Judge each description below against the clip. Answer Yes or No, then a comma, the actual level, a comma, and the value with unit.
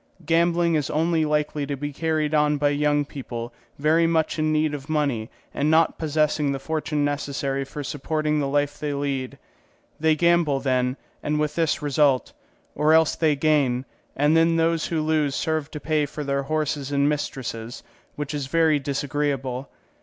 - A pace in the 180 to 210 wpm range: No, average, 170 wpm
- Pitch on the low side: No, medium, 150 Hz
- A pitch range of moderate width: No, narrow, 1.9 semitones